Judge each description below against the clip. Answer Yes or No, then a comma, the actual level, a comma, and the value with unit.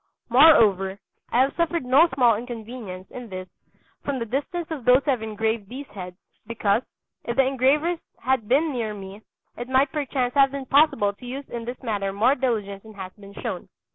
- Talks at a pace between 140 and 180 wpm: No, average, 190 wpm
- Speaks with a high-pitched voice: Yes, high, 245 Hz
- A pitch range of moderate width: Yes, average, 4.5 semitones